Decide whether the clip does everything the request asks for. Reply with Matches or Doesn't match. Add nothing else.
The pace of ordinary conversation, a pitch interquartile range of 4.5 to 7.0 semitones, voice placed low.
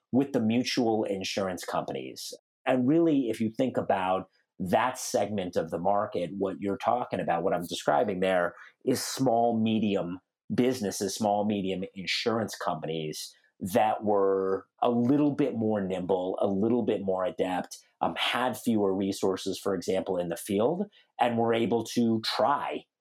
Doesn't match